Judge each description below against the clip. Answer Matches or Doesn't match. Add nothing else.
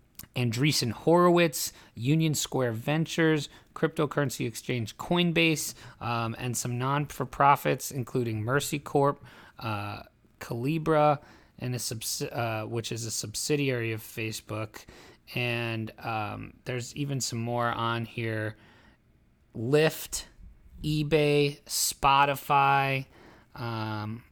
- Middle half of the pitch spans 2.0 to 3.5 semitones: Doesn't match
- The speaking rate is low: Matches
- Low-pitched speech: Matches